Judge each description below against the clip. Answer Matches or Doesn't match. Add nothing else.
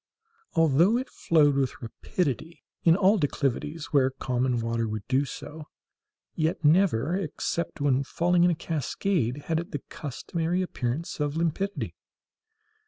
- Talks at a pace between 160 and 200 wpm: Doesn't match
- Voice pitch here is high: Doesn't match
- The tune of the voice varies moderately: Matches